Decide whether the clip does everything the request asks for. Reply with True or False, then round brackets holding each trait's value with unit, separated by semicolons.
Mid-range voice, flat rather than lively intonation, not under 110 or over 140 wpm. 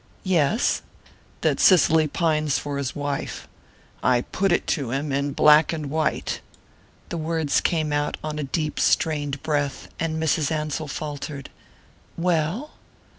True (150 Hz; 2.0 semitones; 135 wpm)